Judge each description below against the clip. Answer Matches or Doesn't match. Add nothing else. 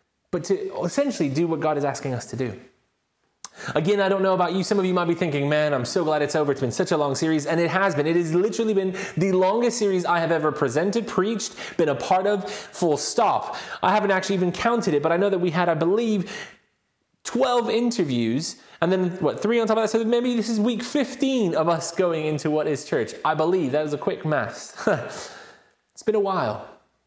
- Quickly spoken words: Matches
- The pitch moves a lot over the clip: Matches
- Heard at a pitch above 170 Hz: Matches